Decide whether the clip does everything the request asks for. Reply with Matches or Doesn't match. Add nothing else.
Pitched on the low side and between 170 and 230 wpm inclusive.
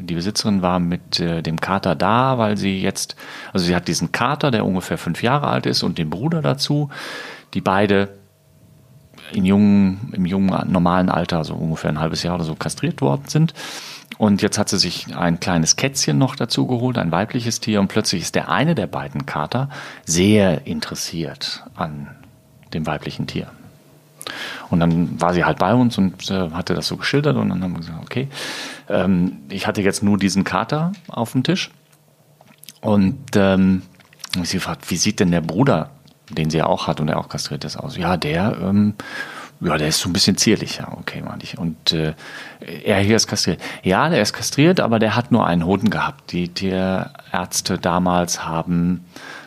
Matches